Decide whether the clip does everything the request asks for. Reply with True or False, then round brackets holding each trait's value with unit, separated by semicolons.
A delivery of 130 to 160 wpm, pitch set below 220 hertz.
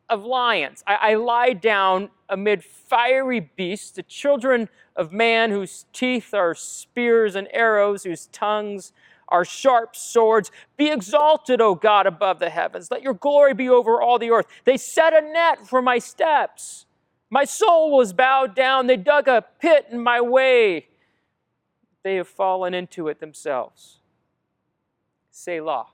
False (150 wpm; 230 Hz)